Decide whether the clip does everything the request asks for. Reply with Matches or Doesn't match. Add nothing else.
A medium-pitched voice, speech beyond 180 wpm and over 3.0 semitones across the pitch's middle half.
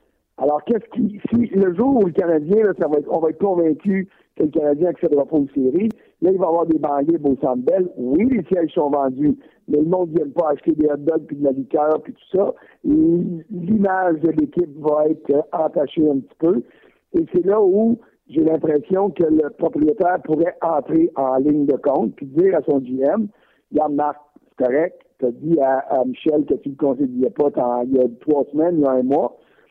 Matches